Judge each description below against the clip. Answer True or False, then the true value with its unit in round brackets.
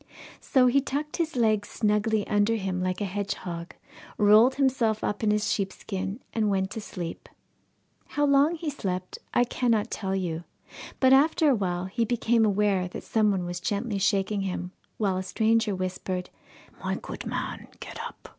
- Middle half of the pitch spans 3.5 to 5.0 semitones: True (3.8 semitones)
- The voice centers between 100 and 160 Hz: False (210 Hz)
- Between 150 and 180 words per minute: True (165 wpm)